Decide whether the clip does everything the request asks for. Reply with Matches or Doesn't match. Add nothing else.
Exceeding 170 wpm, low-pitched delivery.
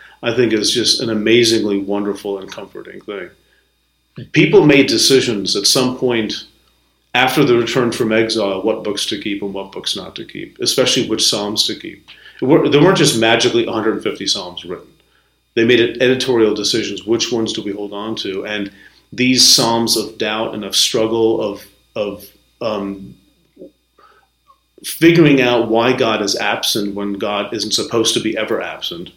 Doesn't match